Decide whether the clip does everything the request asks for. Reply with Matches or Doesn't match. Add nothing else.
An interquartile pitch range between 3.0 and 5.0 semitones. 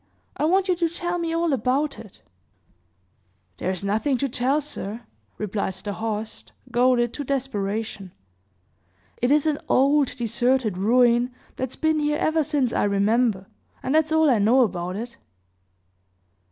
Doesn't match